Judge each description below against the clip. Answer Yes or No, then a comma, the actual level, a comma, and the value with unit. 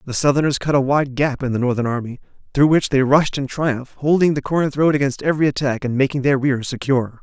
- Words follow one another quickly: Yes, fast, 235 wpm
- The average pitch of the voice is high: No, low, 135 Hz